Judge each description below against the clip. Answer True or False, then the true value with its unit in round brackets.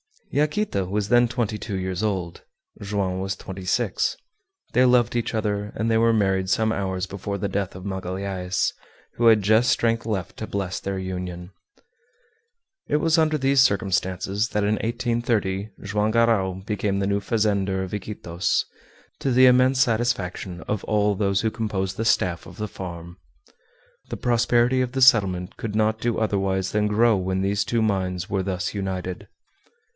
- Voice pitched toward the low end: True (100 Hz)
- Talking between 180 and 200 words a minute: False (165 wpm)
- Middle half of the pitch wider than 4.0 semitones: False (3.2 semitones)